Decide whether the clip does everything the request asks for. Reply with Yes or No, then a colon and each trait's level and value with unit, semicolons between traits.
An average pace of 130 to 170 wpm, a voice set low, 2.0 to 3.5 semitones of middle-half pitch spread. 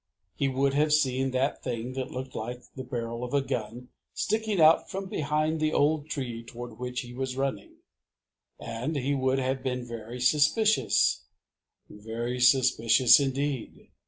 Yes: average, 155 wpm; low, 130 Hz; average, 2.8 semitones